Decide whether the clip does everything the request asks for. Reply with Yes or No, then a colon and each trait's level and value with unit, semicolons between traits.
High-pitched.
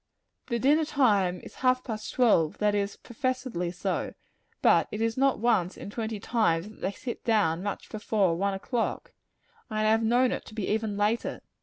Yes: high, 220 Hz